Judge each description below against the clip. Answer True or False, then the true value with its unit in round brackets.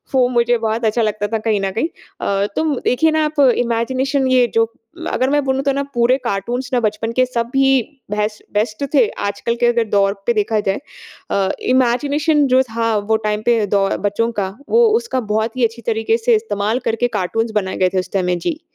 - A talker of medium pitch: False (230 Hz)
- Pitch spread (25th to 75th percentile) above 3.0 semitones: True (3.5 semitones)